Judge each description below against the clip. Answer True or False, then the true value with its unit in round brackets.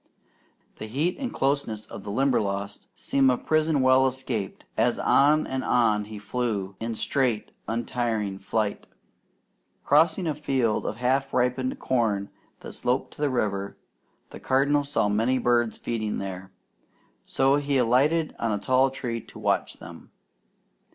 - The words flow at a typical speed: True (145 wpm)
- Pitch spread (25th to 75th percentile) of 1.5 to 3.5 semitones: False (4.1 semitones)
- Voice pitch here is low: True (125 Hz)